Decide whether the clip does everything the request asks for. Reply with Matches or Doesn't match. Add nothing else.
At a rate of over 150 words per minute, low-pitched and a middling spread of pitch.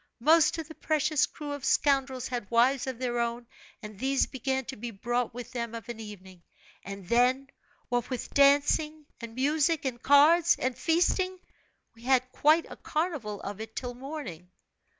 Doesn't match